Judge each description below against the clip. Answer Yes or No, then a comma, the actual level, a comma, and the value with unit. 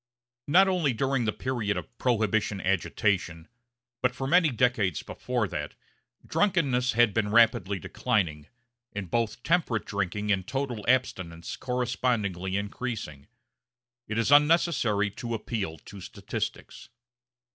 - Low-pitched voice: Yes, low, 110 Hz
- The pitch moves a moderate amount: Yes, average, 4.2 semitones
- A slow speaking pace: Yes, slow, 120 wpm